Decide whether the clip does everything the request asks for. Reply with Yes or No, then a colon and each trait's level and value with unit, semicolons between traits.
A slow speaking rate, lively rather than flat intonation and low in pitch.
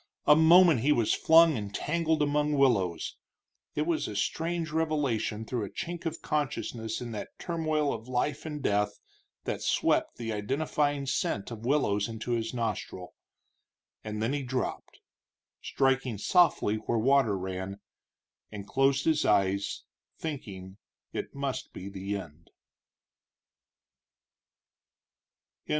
Yes: slow, 130 wpm; wide, 6.2 semitones; low, 125 Hz